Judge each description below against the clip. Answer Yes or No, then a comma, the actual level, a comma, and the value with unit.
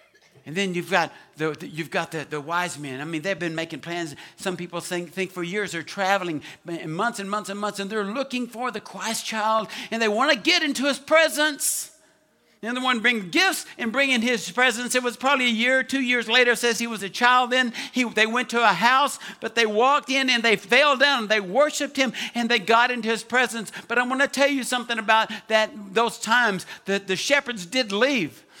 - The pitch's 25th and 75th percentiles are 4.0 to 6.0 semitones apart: Yes, average, 4.5 semitones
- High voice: Yes, high, 230 Hz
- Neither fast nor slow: No, fast, 230 wpm